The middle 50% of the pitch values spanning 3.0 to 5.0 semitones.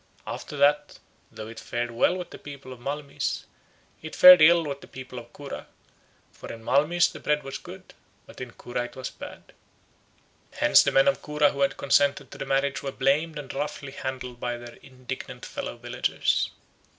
No: narrow, 2.6 semitones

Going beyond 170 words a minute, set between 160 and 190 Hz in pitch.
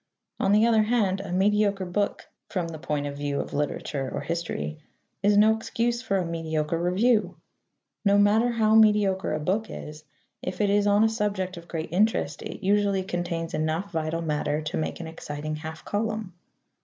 Yes: average, 180 wpm; medium, 185 Hz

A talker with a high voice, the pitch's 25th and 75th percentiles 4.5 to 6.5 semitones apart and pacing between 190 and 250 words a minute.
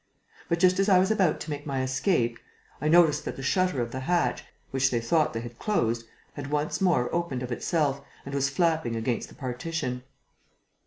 No: medium, 140 Hz; average, 5.3 semitones; average, 200 wpm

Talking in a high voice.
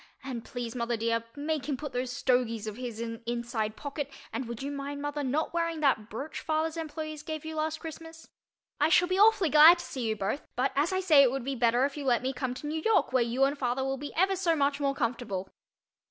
Yes: very high, 275 Hz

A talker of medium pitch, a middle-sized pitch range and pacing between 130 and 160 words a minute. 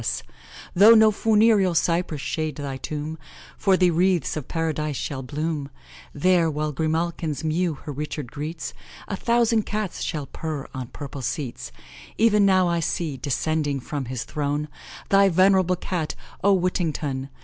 Yes: medium, 160 Hz; average, 4.1 semitones; average, 150 wpm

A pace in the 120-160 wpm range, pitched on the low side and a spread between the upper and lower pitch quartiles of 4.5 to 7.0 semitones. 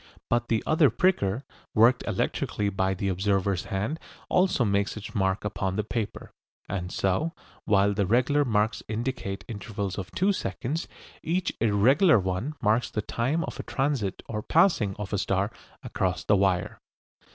Yes: average, 155 wpm; low, 105 Hz; average, 4.8 semitones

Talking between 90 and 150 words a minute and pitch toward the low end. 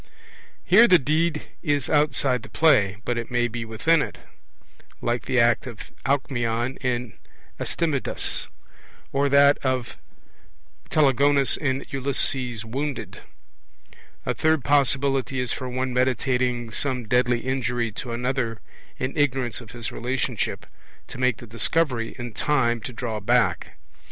Yes: slow, 135 wpm; low, 125 Hz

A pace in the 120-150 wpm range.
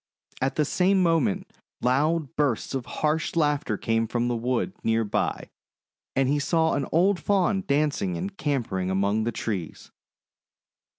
Yes: average, 145 wpm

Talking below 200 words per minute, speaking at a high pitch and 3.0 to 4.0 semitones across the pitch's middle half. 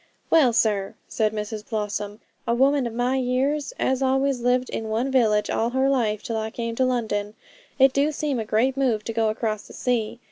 No: fast, 205 wpm; high, 235 Hz; average, 3.3 semitones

